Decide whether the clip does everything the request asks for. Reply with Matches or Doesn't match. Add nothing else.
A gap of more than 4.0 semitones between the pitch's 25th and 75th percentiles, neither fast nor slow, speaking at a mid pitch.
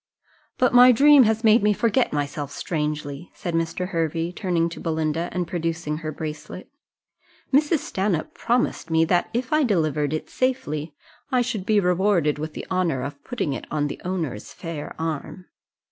Matches